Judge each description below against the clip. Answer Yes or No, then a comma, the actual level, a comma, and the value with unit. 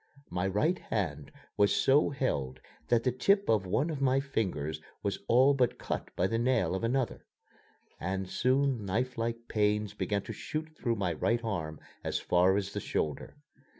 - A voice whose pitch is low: Yes, low, 110 Hz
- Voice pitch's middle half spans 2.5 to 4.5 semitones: No, wide, 5.4 semitones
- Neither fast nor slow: Yes, average, 170 wpm